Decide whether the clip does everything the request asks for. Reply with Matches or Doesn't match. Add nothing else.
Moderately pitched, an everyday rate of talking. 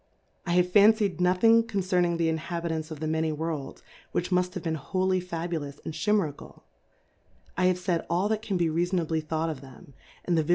Doesn't match